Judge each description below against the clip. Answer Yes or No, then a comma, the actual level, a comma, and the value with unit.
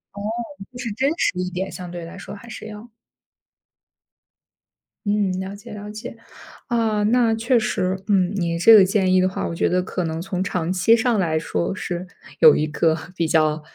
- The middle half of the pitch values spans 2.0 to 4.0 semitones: Yes, average, 3.5 semitones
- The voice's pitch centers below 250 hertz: Yes, high, 190 Hz